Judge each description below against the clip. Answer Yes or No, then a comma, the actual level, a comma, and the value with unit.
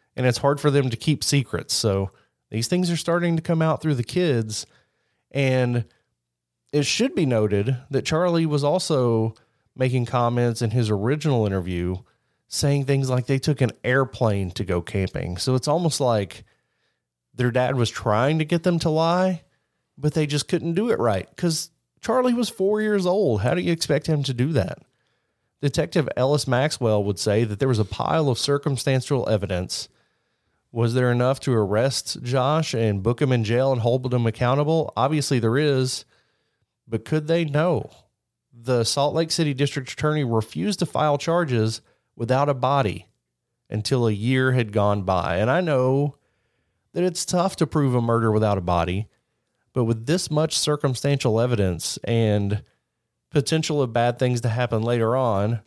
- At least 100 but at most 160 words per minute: No, average, 170 wpm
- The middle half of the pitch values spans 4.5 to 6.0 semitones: Yes, average, 4.9 semitones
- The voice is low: Yes, low, 130 Hz